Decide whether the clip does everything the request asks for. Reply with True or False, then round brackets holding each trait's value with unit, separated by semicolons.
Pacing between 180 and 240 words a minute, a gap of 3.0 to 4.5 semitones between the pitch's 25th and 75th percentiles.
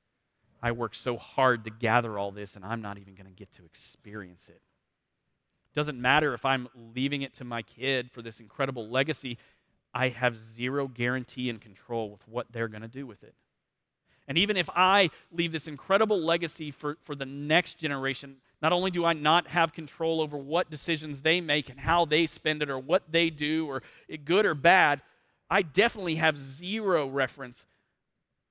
False (185 wpm; 5.2 semitones)